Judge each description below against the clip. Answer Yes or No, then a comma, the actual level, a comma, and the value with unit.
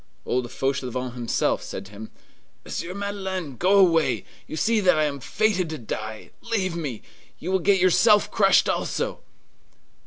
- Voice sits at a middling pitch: Yes, medium, 170 Hz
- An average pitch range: No, wide, 7.2 semitones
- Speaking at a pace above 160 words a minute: No, average, 155 wpm